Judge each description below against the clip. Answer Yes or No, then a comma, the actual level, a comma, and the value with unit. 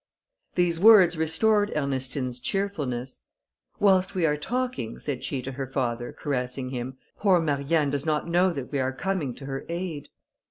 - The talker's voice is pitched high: No, medium, 145 Hz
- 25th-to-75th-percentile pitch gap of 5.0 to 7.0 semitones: Yes, wide, 5.5 semitones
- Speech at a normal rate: Yes, average, 160 wpm